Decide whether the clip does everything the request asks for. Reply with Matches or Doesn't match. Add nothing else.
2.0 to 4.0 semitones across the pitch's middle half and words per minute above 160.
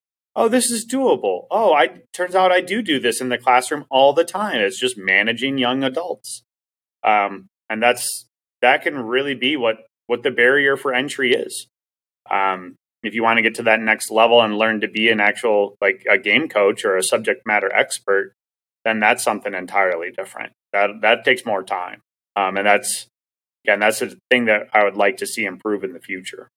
Doesn't match